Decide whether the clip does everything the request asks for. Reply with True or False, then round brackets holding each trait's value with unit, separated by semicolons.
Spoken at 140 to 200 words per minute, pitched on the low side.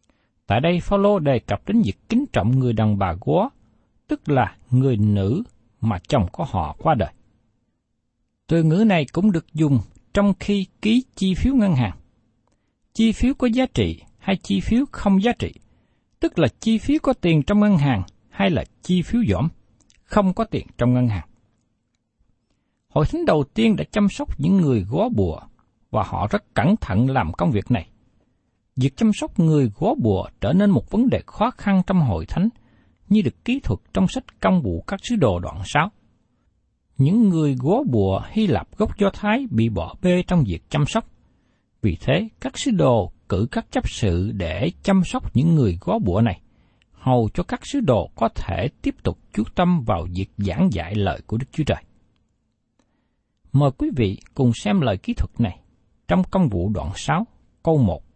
True (190 wpm; 130 Hz)